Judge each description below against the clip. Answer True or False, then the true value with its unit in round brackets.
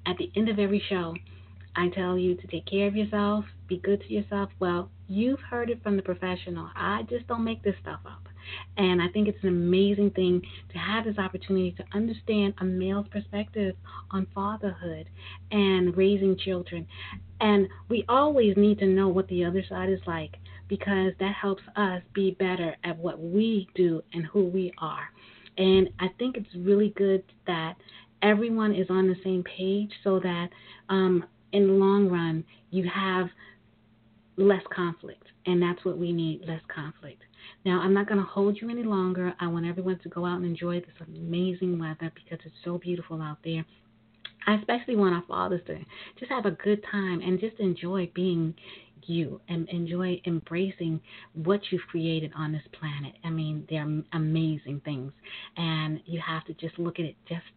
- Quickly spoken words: False (180 wpm)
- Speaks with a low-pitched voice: False (180 Hz)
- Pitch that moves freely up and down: False (3.3 semitones)